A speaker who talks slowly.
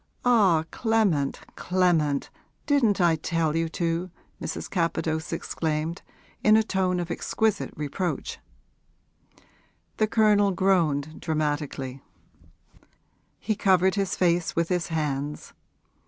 Yes: slow, 105 wpm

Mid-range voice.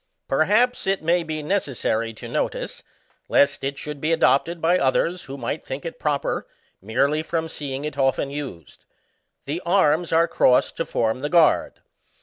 Yes: medium, 150 Hz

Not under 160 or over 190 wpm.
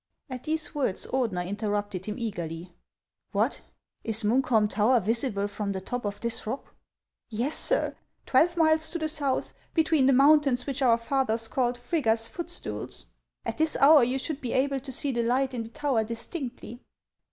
Yes: average, 180 wpm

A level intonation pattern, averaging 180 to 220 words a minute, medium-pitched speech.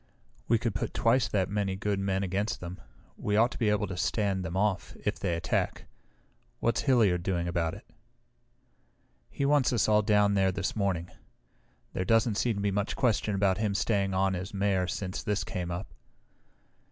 No: narrow, 2.2 semitones; average, 185 wpm; low, 100 Hz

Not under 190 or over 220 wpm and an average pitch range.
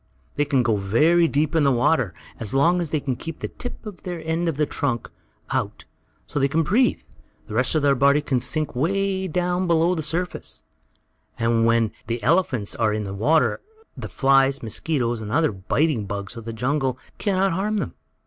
No: average, 195 wpm; wide, 6.0 semitones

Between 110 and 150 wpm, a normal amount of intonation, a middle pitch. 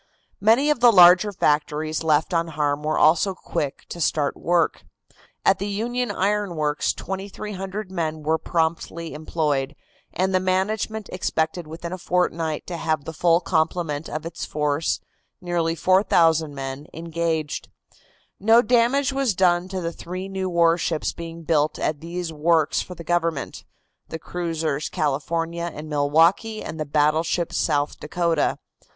Yes: average, 145 wpm; average, 3.1 semitones; medium, 170 Hz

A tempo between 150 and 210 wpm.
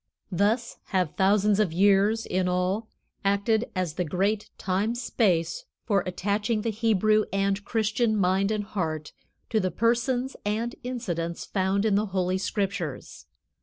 No: average, 140 wpm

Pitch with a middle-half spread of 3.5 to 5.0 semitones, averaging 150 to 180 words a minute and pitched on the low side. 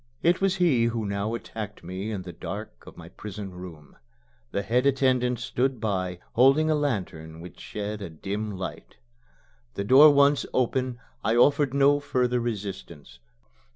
No: wide, 5.5 semitones; average, 155 wpm; low, 115 Hz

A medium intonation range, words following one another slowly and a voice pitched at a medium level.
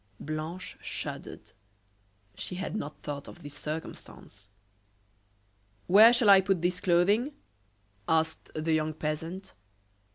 Yes: average, 3.8 semitones; slow, 110 wpm; medium, 170 Hz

